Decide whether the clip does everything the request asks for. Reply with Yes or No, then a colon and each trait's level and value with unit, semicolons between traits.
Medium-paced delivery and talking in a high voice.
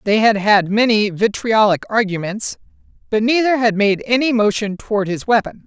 Yes: average, 160 wpm; high, 215 Hz